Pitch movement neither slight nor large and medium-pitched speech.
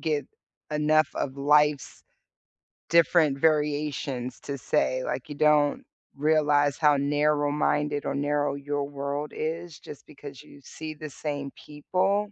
No: narrow, 1.2 semitones; medium, 145 Hz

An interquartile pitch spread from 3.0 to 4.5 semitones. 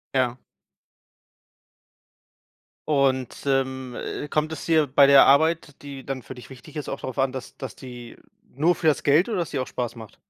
No: narrow, 2.6 semitones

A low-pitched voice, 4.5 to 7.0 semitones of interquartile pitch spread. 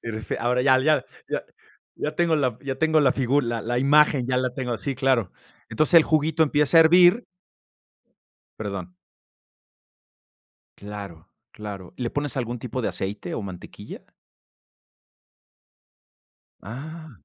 Yes: low, 130 Hz; average, 5.3 semitones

